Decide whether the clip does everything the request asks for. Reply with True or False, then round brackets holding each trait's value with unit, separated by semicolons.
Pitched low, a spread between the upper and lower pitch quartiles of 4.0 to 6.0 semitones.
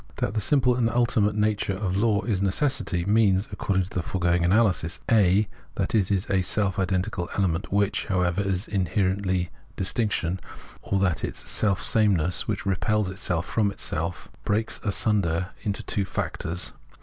False (100 Hz; 2.7 semitones)